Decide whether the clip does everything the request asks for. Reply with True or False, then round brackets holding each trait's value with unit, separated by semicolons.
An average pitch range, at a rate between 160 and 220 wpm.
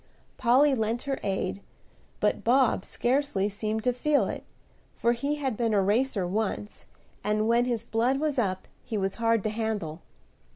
True (3.5 semitones; 165 wpm)